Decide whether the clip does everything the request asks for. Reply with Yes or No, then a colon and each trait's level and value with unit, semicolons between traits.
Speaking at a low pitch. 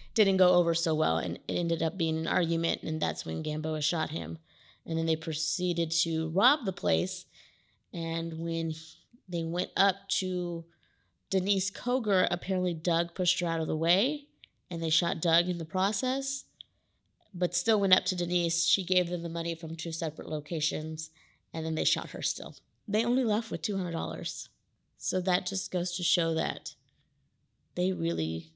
No: medium, 170 Hz